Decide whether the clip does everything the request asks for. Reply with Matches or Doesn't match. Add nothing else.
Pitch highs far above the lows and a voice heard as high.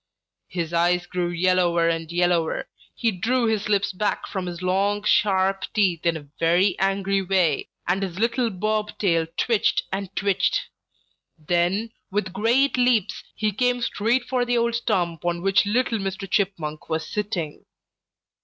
Doesn't match